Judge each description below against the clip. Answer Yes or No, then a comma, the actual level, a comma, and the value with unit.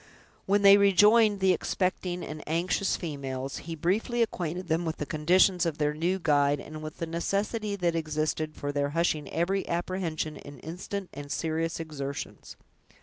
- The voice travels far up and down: No, average, 3.6 semitones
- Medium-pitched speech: Yes, medium, 165 Hz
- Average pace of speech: Yes, average, 160 wpm